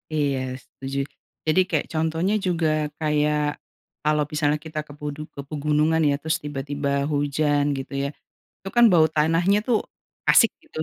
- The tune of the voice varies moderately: No, narrow, 1.9 semitones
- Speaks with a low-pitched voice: No, medium, 150 Hz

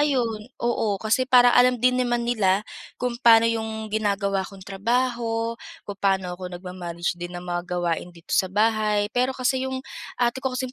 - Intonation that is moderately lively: Yes, average, 4.3 semitones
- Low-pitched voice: No, high, 220 Hz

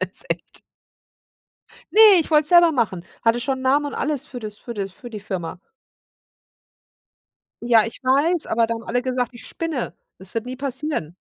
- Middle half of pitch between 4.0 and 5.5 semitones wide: Yes, average, 4.4 semitones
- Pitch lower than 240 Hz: No, high, 245 Hz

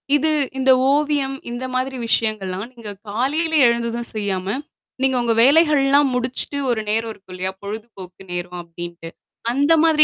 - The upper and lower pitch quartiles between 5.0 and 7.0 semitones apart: Yes, wide, 5.5 semitones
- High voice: Yes, high, 235 Hz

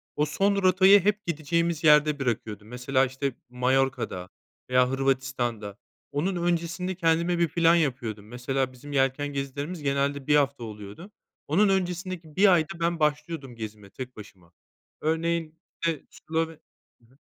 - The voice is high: No, medium, 145 Hz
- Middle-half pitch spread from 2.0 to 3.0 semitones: No, average, 4.9 semitones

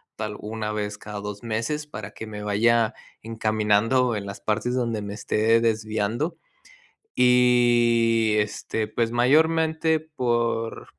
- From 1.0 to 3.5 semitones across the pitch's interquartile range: Yes, narrow, 2.4 semitones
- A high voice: No, low, 115 Hz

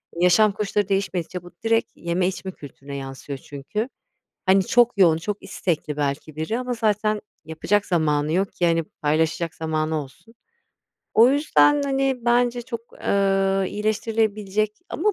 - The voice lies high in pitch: Yes, high, 195 Hz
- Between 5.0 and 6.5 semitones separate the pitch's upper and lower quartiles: Yes, wide, 5.4 semitones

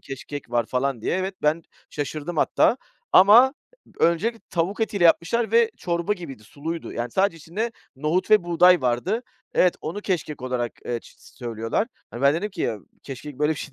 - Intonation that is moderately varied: No, wide, 6.0 semitones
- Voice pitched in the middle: Yes, medium, 165 Hz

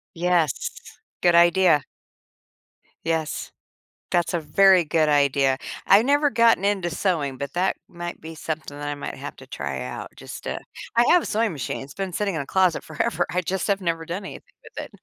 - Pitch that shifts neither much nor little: Yes, average, 4.3 semitones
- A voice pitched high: No, medium, 170 Hz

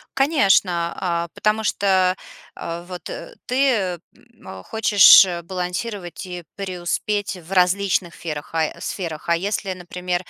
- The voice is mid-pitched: Yes, medium, 180 Hz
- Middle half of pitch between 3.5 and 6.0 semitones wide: No, narrow, 2.6 semitones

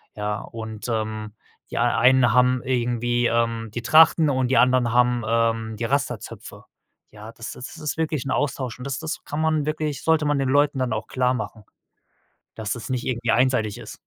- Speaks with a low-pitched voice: Yes, low, 125 Hz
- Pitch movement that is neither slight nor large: Yes, average, 3.1 semitones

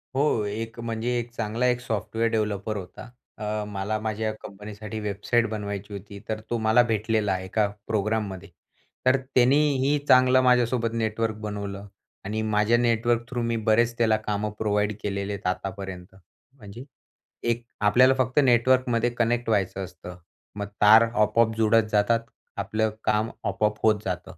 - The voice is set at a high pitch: No, low, 110 Hz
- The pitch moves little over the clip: Yes, narrow, 2.3 semitones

